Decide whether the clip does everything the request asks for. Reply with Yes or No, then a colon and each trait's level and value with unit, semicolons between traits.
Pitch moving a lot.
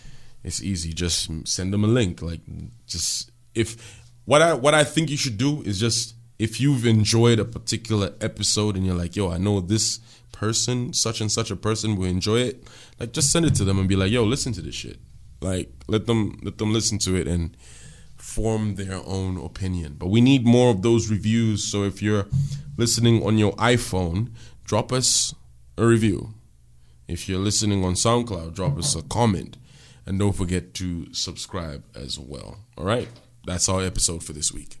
No: average, 4.1 semitones